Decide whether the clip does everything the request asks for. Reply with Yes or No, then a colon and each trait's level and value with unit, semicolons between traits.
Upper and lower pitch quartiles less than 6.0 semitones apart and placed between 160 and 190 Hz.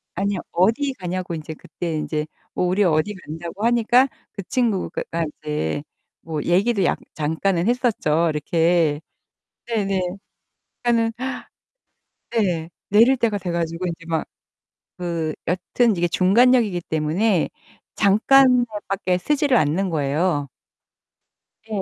Yes: wide, 5.4 semitones; medium, 185 Hz